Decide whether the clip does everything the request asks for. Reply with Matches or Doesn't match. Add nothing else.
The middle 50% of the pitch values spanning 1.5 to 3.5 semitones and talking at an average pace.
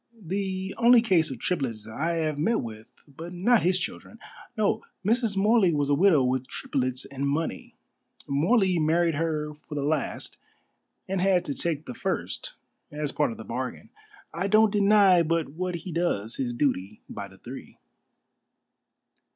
Doesn't match